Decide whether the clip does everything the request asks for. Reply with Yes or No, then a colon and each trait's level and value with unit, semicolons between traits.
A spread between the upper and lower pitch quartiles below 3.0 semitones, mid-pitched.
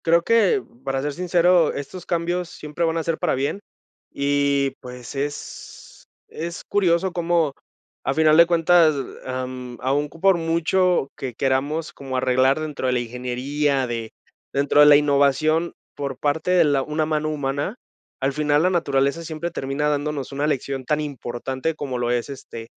No: average, 3.5 semitones; medium, 145 Hz